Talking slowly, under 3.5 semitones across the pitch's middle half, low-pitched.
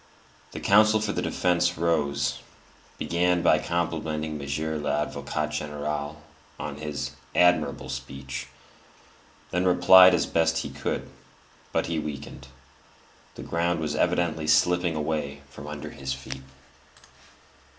Yes: slow, 120 wpm; average, 3.0 semitones; very low, 75 Hz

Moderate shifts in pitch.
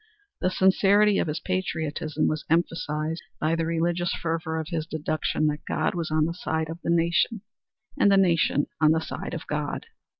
No: narrow, 1.9 semitones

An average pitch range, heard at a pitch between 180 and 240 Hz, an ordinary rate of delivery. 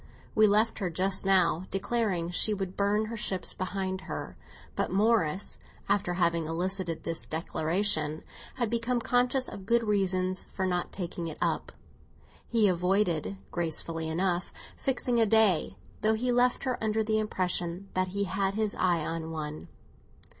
Yes: average, 3.9 semitones; high, 190 Hz; average, 155 wpm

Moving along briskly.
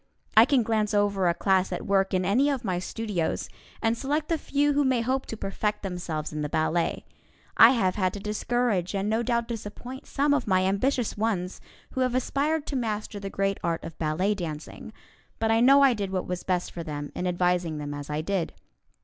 Yes: fast, 210 wpm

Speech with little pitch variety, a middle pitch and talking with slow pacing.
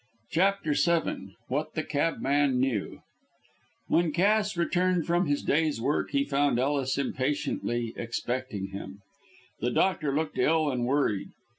No: average, 4.5 semitones; medium, 145 Hz; slow, 130 wpm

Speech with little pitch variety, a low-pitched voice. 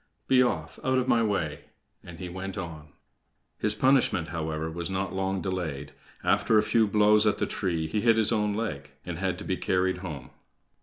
No: average, 4.2 semitones; very low, 95 Hz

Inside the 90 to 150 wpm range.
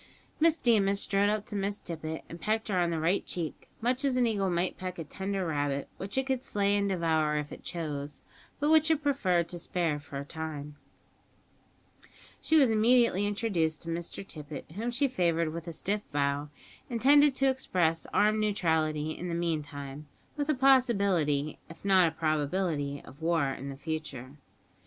No: average, 180 wpm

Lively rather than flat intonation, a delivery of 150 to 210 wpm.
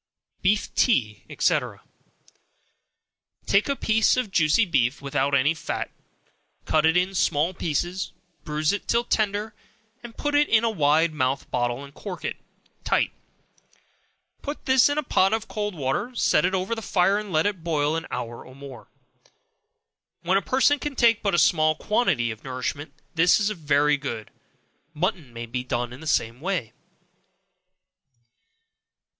Yes: wide, 6.9 semitones; average, 155 wpm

